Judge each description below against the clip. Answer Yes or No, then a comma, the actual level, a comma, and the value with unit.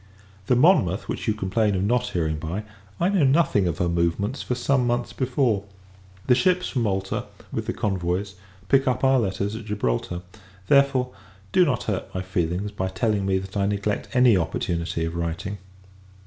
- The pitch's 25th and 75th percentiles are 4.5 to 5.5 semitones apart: Yes, average, 5.2 semitones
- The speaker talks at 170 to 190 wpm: Yes, average, 175 wpm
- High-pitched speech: No, low, 105 Hz